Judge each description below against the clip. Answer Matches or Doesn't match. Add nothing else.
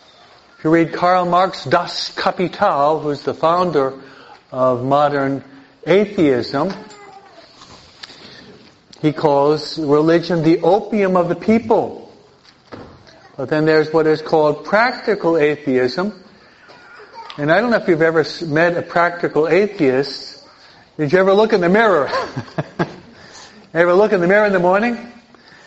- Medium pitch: Matches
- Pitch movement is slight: Doesn't match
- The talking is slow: Matches